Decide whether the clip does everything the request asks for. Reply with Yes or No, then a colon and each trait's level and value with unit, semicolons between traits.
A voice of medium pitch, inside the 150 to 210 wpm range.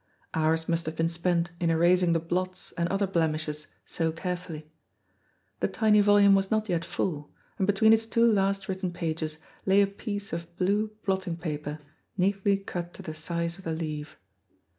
Yes: medium, 175 Hz; average, 175 wpm